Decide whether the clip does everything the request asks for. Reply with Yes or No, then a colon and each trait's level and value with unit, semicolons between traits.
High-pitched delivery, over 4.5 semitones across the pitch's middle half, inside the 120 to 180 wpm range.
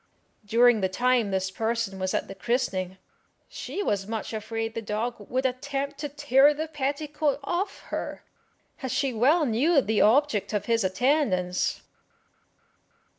Yes: high, 240 Hz; average, 5.2 semitones; average, 145 wpm